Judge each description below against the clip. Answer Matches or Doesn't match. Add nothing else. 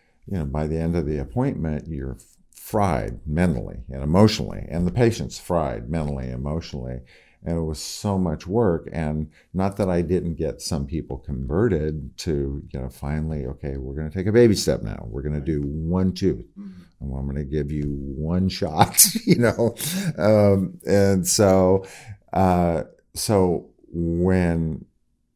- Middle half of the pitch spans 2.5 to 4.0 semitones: Doesn't match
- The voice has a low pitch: Matches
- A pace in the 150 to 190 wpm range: Matches